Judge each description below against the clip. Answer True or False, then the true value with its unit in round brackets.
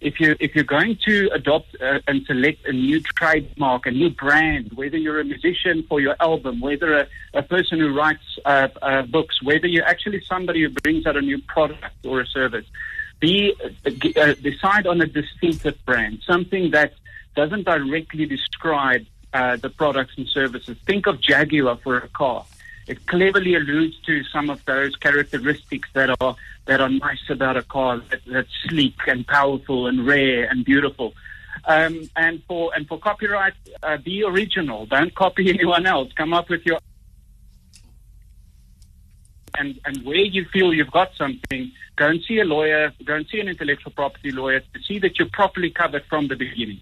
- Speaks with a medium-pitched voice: True (150 Hz)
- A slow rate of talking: False (180 wpm)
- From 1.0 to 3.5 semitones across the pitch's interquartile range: False (4.0 semitones)